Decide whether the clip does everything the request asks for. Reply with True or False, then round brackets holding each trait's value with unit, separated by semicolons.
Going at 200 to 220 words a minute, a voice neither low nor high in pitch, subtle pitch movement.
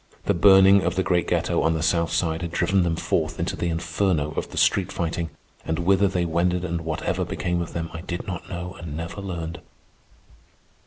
False (205 wpm; 85 Hz; 1.8 semitones)